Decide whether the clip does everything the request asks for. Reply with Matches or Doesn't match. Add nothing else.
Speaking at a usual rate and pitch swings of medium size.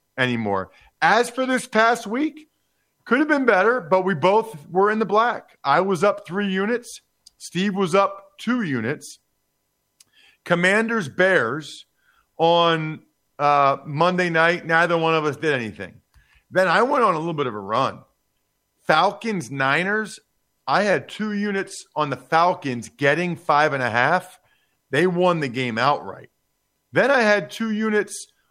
Doesn't match